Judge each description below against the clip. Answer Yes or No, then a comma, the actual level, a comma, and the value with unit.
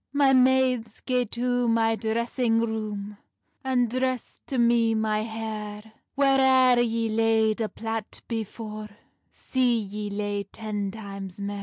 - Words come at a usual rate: No, slow, 130 wpm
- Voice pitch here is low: No, high, 225 Hz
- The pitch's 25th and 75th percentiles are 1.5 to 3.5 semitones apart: Yes, narrow, 2.5 semitones